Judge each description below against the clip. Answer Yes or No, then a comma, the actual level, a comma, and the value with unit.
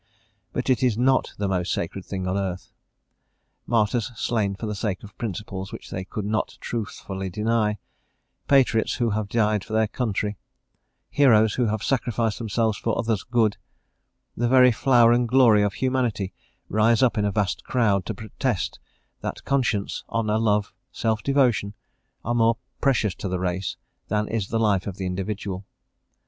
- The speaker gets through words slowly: No, average, 165 wpm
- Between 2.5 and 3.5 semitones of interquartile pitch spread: Yes, average, 2.9 semitones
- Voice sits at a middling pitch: No, low, 110 Hz